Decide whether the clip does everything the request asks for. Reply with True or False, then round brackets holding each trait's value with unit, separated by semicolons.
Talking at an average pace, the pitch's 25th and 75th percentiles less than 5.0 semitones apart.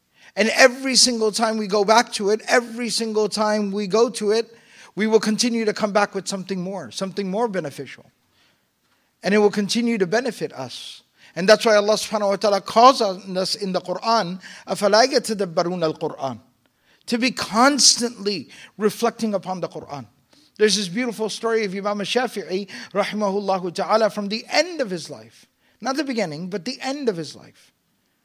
True (170 wpm; 3.1 semitones)